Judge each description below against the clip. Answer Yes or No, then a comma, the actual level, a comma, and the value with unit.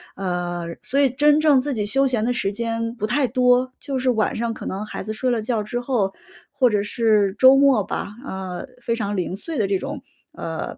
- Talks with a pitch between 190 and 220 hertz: No, high, 230 Hz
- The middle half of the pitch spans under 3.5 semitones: No, average, 4.1 semitones